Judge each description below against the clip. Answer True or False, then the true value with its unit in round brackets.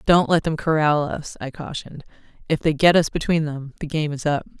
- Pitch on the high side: False (155 Hz)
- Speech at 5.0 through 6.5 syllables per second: True (5.5 syllables/s)